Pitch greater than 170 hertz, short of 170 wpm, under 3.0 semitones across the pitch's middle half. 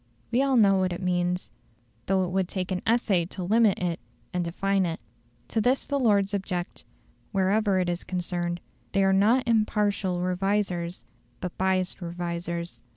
Yes: high, 190 Hz; average, 160 wpm; narrow, 2.5 semitones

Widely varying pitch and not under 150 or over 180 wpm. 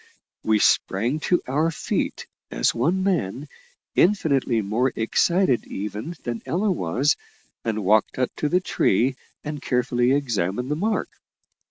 No: wide, 6.2 semitones; slow, 135 wpm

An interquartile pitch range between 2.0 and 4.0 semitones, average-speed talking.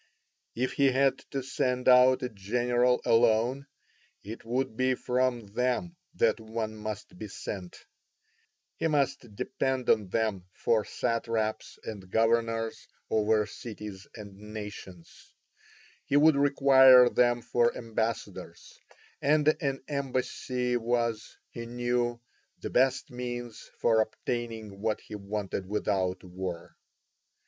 No: average, 2.9 semitones; slow, 120 wpm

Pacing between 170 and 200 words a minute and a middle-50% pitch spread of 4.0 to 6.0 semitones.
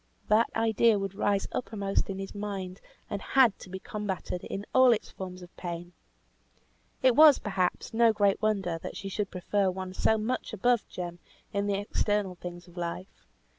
No: average, 175 wpm; average, 2.8 semitones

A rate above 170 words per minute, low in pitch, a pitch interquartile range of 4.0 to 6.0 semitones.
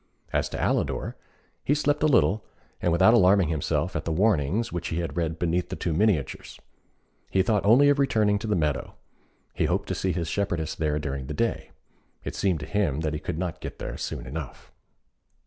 Yes: average, 200 wpm; very low, 90 Hz; average, 5.1 semitones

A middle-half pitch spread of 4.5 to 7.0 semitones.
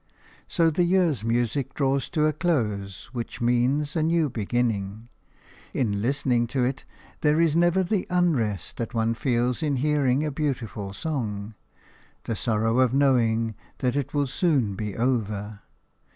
Yes: average, 4.9 semitones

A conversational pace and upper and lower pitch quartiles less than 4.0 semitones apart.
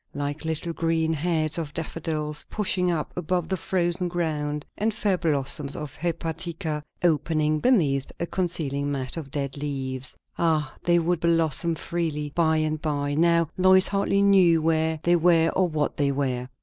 Yes: average, 160 wpm; average, 2.7 semitones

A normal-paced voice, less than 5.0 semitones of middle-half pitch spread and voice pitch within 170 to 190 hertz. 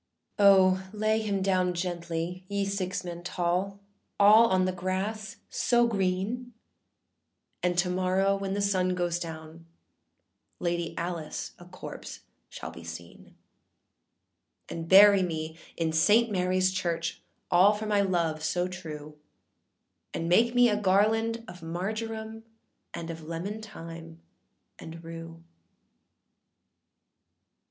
No: slow, 125 wpm; average, 3.2 semitones; medium, 185 Hz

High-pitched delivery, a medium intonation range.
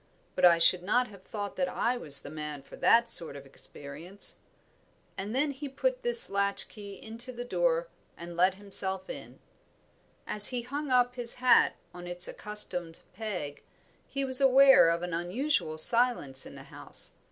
No: high, 205 Hz; wide, 6.3 semitones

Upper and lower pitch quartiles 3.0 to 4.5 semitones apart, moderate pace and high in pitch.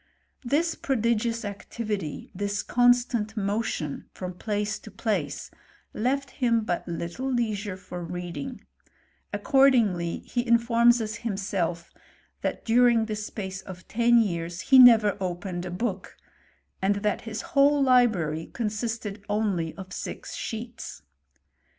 No: average, 4.2 semitones; slow, 125 wpm; high, 215 Hz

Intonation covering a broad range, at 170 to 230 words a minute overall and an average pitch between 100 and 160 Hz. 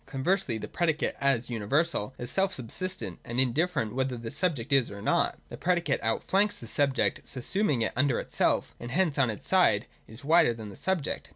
Yes: wide, 6.5 semitones; average, 190 wpm; low, 135 Hz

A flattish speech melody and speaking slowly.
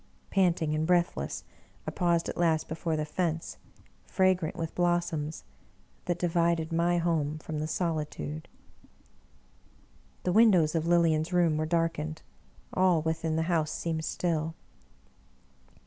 Yes: narrow, 1.7 semitones; slow, 125 wpm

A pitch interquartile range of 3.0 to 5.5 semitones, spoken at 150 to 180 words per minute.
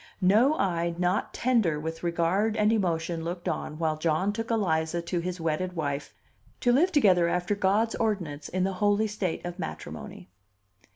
Yes: average, 4.1 semitones; average, 165 wpm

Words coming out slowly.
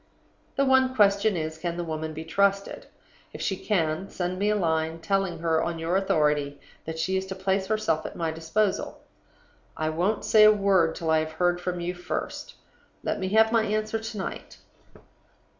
No: average, 190 wpm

